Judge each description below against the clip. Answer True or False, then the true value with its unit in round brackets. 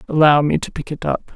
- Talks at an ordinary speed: False (265 wpm)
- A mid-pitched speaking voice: True (150 Hz)